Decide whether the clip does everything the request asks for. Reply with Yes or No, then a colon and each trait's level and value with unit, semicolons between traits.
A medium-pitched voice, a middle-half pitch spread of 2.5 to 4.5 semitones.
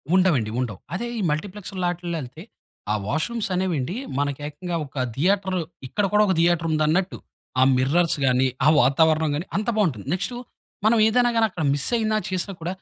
No: medium, 175 Hz; average, 5.0 semitones